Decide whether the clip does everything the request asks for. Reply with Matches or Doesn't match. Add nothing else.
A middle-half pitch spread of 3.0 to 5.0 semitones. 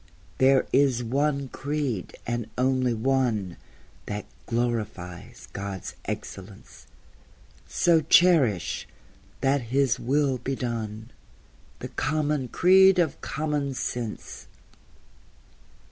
Matches